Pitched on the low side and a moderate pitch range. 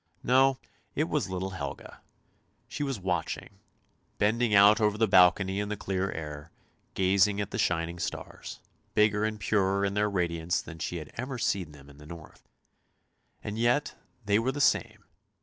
Yes: low, 100 Hz; average, 3.6 semitones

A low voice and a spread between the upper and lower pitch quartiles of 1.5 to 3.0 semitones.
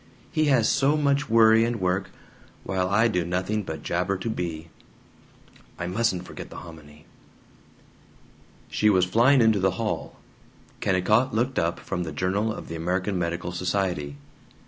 No: very low, 95 Hz; average, 4.2 semitones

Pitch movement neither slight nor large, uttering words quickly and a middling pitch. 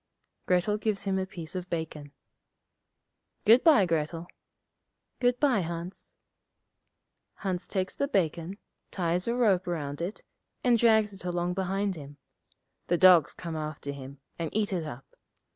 No: average, 3.7 semitones; average, 145 wpm; medium, 180 Hz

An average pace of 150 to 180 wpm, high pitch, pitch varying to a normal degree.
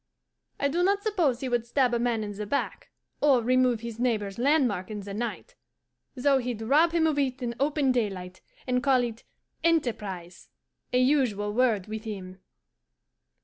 Yes: average, 170 wpm; high, 245 Hz; average, 4.5 semitones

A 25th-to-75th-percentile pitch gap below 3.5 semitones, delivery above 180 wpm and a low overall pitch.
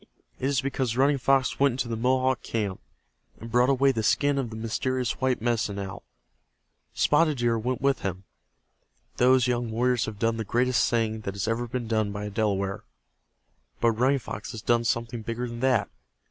Yes: average, 2.7 semitones; average, 190 wpm; low, 120 Hz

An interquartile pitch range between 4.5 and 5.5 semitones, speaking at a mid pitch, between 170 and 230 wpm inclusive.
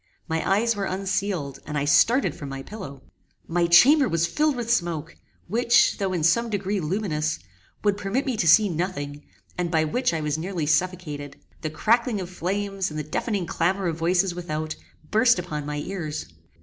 Yes: average, 4.9 semitones; medium, 175 Hz; average, 180 wpm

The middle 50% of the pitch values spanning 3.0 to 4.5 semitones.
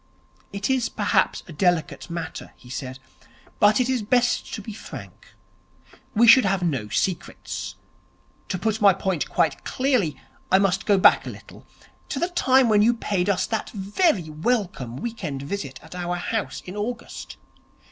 No: average, 4.9 semitones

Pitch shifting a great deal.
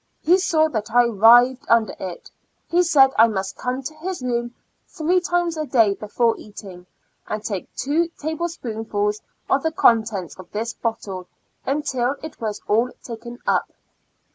Yes: wide, 6.2 semitones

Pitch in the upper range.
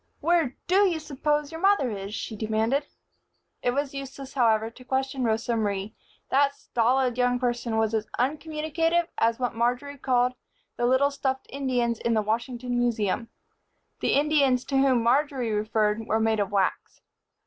Yes: very high, 250 Hz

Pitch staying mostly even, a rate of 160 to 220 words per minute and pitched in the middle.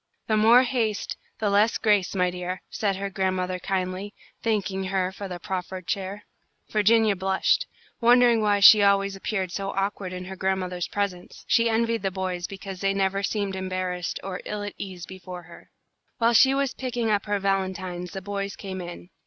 No: narrow, 2.1 semitones; average, 180 wpm; high, 195 Hz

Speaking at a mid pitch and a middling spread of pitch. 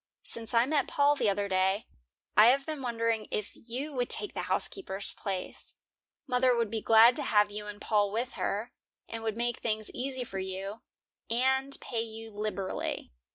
No: high, 225 Hz; average, 3.3 semitones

